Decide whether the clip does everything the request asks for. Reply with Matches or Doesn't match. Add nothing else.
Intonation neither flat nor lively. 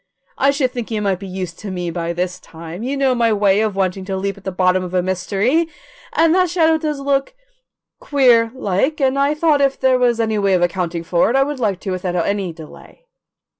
Doesn't match